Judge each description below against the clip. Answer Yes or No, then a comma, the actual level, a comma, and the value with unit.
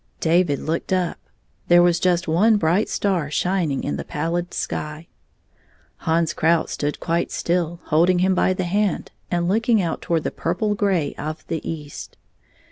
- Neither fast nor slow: Yes, average, 160 wpm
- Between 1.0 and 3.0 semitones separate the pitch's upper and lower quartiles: Yes, narrow, 2.4 semitones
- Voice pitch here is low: No, medium, 170 Hz